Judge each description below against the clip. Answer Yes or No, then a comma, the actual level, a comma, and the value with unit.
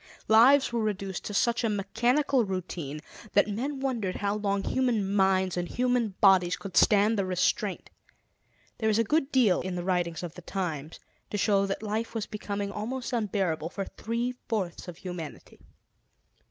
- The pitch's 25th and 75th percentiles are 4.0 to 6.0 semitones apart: No, average, 3.6 semitones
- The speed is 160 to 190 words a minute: Yes, average, 165 wpm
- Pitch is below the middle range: No, high, 205 Hz